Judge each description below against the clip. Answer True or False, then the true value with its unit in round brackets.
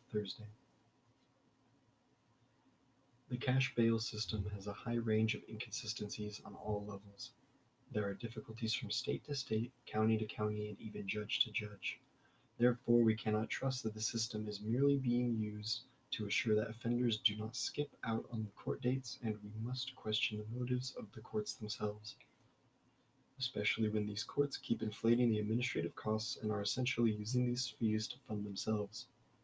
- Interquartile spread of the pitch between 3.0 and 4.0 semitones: False (2.6 semitones)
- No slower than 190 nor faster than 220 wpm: False (165 wpm)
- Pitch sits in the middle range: False (115 Hz)